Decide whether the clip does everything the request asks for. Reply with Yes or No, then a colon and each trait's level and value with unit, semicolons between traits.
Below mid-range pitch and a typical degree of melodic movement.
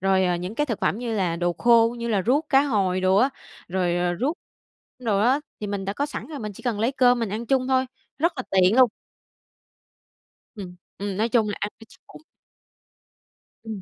No: high, 220 Hz; average, 4.9 semitones